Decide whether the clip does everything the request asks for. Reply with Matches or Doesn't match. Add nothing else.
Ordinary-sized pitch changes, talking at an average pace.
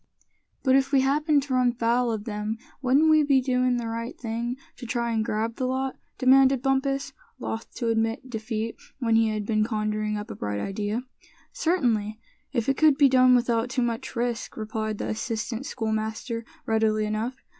Matches